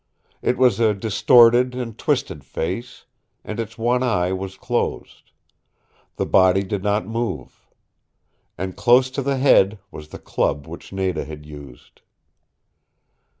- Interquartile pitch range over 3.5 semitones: Yes, average, 4.7 semitones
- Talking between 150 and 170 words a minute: No, slow, 135 wpm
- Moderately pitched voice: No, low, 105 Hz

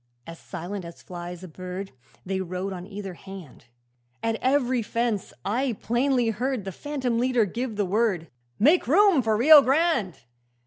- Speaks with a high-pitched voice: Yes, high, 220 Hz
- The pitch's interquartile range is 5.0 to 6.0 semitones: Yes, wide, 5.5 semitones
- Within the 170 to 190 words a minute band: No, average, 160 wpm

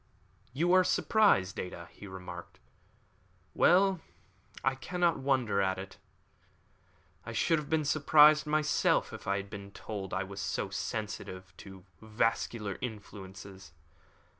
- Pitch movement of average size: No, wide, 7.8 semitones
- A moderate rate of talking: No, slow, 130 wpm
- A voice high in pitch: No, low, 105 Hz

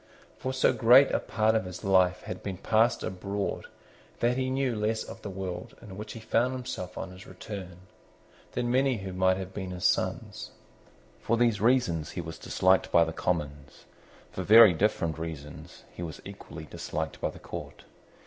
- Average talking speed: Yes, average, 180 wpm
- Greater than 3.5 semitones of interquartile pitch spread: Yes, average, 4.2 semitones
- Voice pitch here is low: Yes, very low, 95 Hz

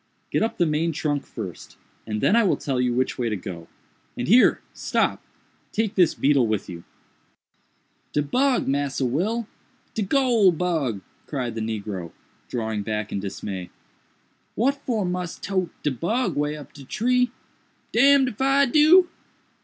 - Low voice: No, medium, 155 Hz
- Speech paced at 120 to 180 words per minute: Yes, average, 145 wpm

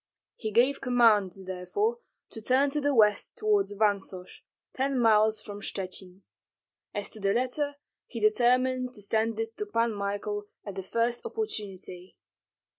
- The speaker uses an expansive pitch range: No, average, 3.9 semitones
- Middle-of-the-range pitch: No, high, 220 Hz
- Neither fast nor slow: Yes, average, 145 wpm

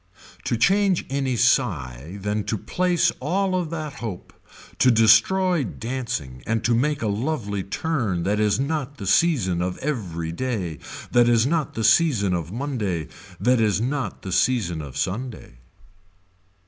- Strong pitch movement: Yes, wide, 6.8 semitones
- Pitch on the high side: No, low, 115 Hz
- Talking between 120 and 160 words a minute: Yes, average, 150 wpm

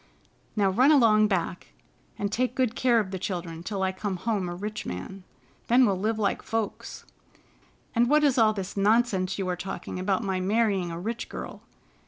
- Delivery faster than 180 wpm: Yes, average, 190 wpm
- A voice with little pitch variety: No, average, 3.4 semitones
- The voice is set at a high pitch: Yes, high, 205 Hz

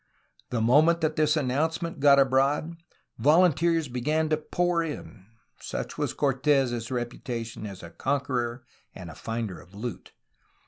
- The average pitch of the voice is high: No, low, 135 Hz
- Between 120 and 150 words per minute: Yes, average, 140 wpm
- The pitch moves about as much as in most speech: Yes, average, 4.7 semitones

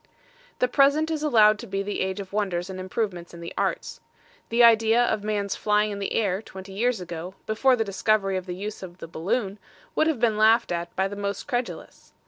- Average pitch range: Yes, average, 3.1 semitones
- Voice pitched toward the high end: Yes, high, 205 Hz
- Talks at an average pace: No, fast, 215 wpm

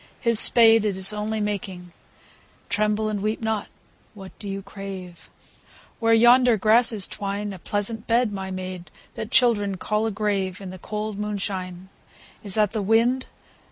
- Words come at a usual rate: Yes, average, 170 wpm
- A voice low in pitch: No, high, 210 Hz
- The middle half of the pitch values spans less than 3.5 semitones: Yes, narrow, 2.4 semitones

